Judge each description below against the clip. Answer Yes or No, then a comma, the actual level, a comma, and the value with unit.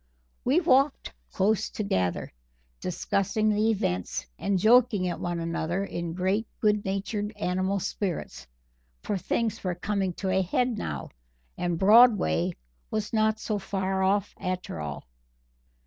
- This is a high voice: Yes, high, 195 Hz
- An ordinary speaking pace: No, slow, 130 wpm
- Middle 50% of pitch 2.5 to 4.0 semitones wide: Yes, average, 3.2 semitones